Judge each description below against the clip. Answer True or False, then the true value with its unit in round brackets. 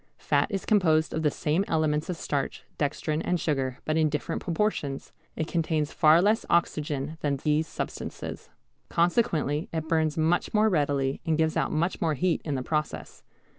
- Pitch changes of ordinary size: False (2.2 semitones)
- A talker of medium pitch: True (155 Hz)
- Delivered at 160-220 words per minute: True (170 wpm)